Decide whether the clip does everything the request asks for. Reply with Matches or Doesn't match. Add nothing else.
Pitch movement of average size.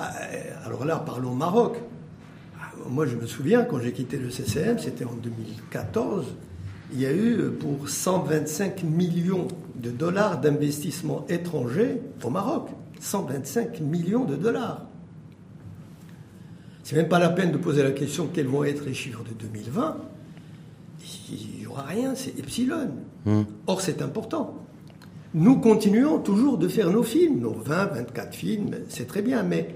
Doesn't match